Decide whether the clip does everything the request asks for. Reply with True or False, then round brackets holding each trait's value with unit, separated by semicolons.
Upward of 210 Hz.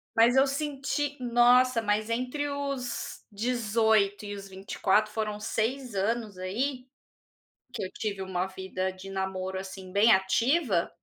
True (220 Hz)